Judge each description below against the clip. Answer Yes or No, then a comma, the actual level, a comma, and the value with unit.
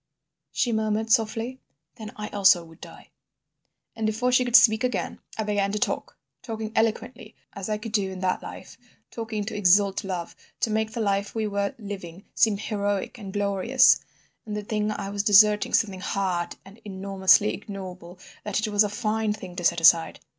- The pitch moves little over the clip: Yes, narrow, 2.0 semitones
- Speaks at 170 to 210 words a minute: Yes, average, 175 wpm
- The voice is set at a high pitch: Yes, high, 210 Hz